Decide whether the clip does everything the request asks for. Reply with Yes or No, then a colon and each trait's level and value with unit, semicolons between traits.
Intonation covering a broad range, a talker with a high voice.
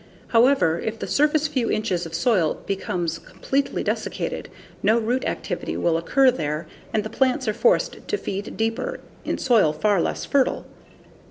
Yes: wide, 6.8 semitones; high, 220 Hz